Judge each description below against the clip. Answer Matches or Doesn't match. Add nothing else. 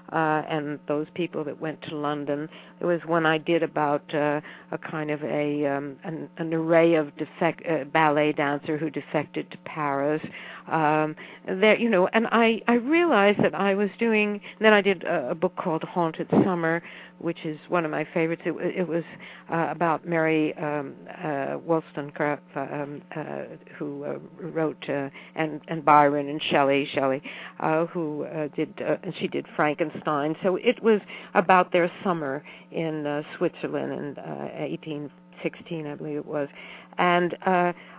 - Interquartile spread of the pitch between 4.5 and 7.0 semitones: Doesn't match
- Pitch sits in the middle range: Matches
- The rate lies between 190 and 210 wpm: Doesn't match